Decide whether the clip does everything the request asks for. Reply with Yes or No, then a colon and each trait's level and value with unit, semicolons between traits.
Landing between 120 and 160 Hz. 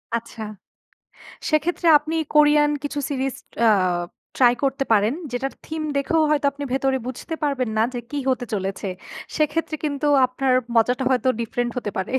No: very high, 270 Hz